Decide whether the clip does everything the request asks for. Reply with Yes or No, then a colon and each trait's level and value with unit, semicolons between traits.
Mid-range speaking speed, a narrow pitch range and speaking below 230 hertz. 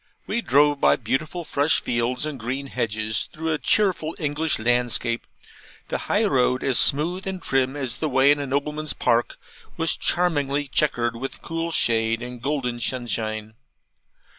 No: average, 155 wpm; average, 4.3 semitones; low, 135 Hz